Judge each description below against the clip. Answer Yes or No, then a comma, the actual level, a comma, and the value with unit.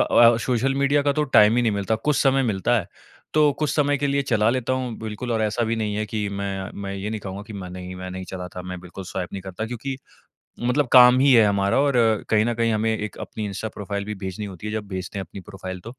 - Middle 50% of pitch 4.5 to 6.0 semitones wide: No, average, 4.1 semitones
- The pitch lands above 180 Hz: No, low, 110 Hz